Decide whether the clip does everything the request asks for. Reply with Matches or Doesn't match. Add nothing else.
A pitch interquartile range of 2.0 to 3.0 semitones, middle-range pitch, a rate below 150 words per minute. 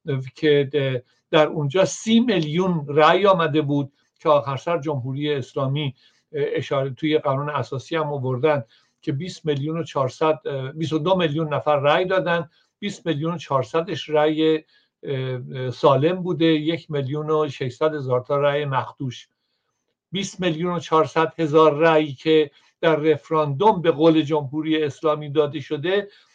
Matches